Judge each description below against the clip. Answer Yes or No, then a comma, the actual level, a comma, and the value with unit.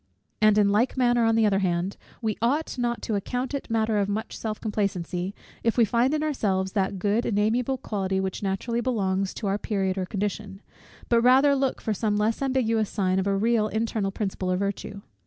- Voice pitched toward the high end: Yes, high, 215 Hz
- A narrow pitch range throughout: No, average, 3.2 semitones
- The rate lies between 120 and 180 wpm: No, fast, 205 wpm